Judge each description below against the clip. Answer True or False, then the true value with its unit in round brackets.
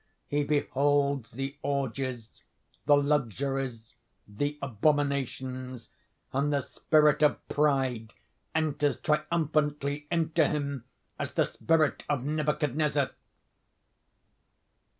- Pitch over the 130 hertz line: True (140 Hz)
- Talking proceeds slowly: True (90 wpm)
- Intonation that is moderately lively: False (2.1 semitones)